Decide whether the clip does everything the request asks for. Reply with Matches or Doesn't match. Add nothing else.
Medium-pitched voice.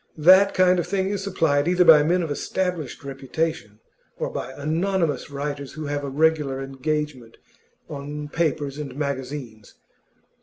Matches